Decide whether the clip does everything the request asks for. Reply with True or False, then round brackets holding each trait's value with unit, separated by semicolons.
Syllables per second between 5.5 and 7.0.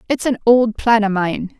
False (4.5 syllables/s)